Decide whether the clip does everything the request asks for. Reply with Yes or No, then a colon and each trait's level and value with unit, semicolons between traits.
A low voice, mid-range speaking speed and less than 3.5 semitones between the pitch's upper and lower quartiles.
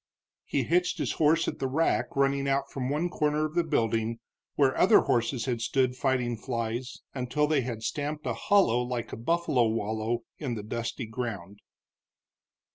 No: low, 130 Hz; average, 170 wpm; average, 4.3 semitones